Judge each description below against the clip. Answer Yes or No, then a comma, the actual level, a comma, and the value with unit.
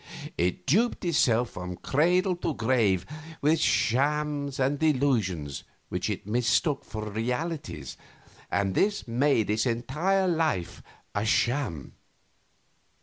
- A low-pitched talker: Yes, low, 130 Hz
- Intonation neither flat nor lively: No, wide, 6.2 semitones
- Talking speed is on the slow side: Yes, slow, 110 wpm